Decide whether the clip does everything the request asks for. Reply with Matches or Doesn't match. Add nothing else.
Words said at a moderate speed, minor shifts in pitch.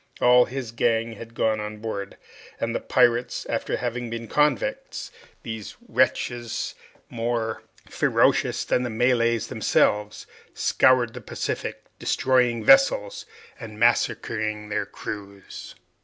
Doesn't match